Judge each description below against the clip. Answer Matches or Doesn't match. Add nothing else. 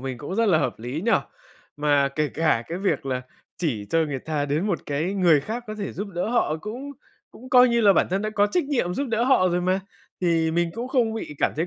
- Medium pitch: Matches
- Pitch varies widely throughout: Matches